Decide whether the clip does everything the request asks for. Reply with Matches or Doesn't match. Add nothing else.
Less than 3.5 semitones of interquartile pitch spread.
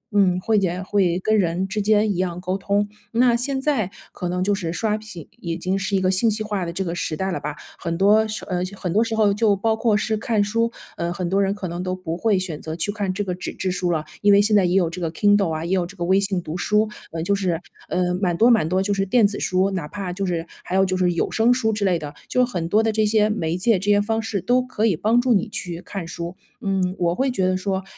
Matches